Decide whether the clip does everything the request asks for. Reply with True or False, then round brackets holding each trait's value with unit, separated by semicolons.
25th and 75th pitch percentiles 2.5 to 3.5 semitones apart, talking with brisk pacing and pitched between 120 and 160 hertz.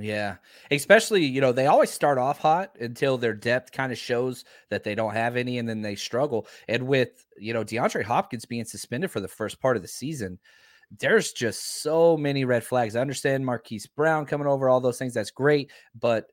True (3.1 semitones; 210 wpm; 125 Hz)